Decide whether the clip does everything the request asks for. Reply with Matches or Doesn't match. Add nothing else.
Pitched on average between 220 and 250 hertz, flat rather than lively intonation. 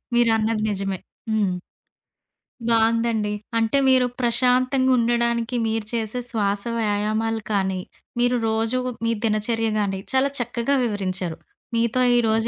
Matches